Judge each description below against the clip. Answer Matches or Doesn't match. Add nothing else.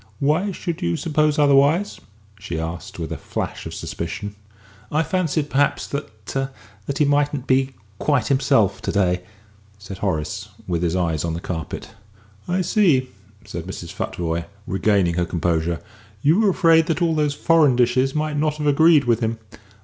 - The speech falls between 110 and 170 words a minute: Matches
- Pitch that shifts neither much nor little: Doesn't match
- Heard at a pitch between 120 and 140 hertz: Matches